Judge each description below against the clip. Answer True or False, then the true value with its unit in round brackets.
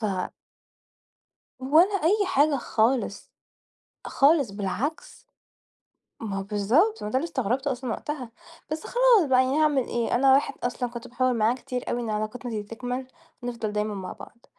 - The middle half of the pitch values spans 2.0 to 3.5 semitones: False (4.3 semitones)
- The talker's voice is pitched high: True (250 Hz)